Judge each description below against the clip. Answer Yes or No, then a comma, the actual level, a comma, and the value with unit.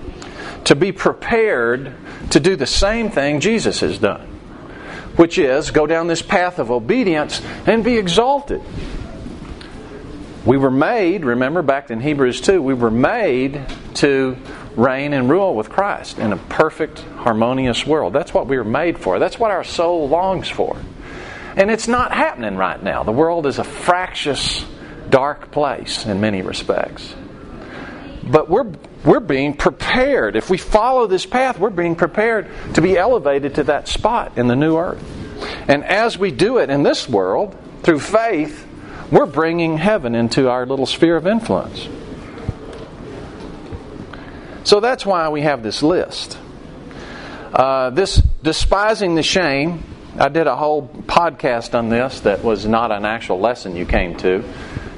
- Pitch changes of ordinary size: No, wide, 6.8 semitones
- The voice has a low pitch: No, medium, 150 Hz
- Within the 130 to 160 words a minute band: Yes, average, 155 wpm